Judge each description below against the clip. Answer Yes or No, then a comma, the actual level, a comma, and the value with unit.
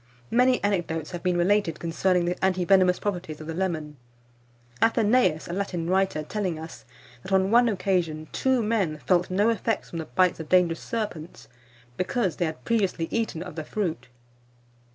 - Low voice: No, medium, 180 Hz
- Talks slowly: No, average, 170 wpm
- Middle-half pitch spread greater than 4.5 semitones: No, average, 3.8 semitones